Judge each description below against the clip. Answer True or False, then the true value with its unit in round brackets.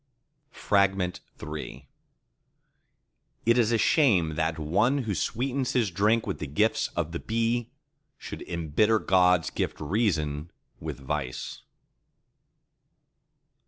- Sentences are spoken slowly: True (105 wpm)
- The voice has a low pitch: True (95 Hz)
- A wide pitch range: True (6.1 semitones)